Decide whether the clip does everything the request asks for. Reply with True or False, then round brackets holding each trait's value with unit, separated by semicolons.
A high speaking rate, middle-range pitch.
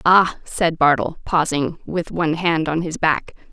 False (170 wpm; 165 Hz)